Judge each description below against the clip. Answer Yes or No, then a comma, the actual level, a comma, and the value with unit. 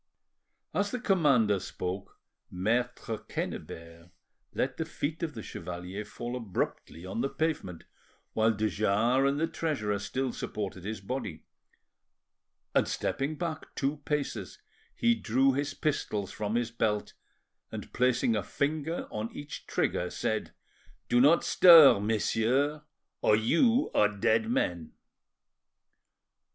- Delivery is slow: Yes, slow, 125 wpm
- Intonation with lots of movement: Yes, wide, 5.9 semitones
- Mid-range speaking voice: No, low, 120 Hz